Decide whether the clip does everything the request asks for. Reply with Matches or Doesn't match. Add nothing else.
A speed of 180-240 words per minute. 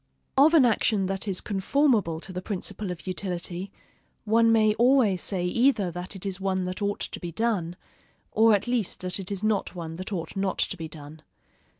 Matches